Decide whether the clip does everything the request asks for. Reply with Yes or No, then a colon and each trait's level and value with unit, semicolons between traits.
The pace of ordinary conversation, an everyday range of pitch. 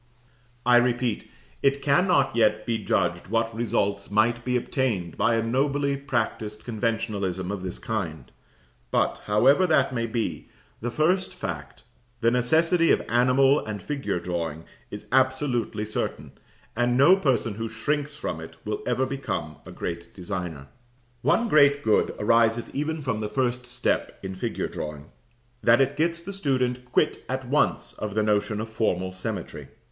Yes: average, 155 wpm; average, 4.5 semitones